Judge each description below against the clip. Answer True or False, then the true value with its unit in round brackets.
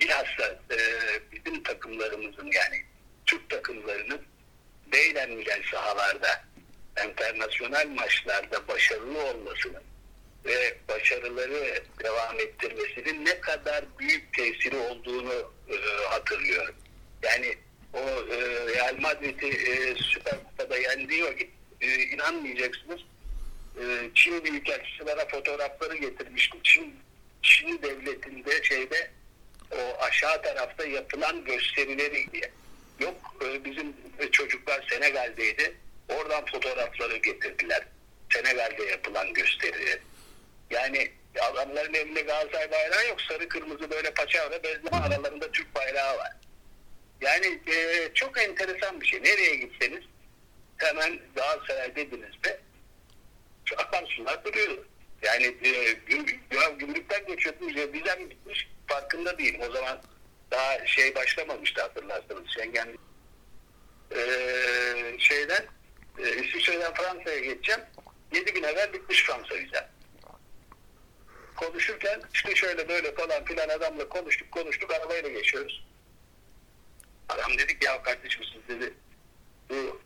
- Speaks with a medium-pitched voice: False (240 Hz)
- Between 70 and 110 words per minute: True (105 wpm)